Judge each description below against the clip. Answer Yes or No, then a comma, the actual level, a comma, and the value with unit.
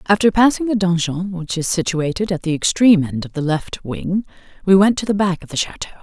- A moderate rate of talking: No, fast, 230 wpm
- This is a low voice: No, medium, 185 Hz